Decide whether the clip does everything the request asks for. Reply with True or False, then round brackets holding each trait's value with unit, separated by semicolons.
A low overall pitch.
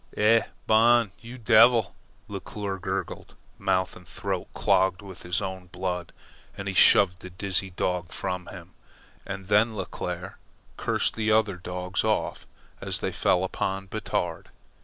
True (95 Hz)